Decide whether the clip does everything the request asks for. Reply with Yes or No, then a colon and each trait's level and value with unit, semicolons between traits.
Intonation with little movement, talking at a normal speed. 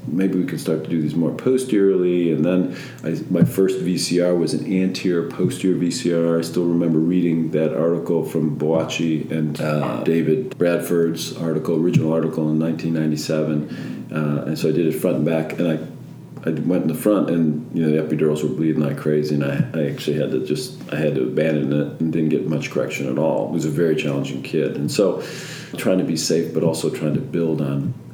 No: narrow, 1.7 semitones; fast, 210 wpm